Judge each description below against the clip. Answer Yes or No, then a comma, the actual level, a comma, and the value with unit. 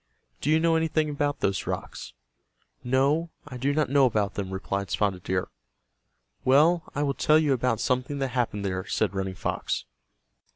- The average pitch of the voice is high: No, low, 130 Hz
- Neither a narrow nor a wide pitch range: No, wide, 6.7 semitones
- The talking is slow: No, average, 170 wpm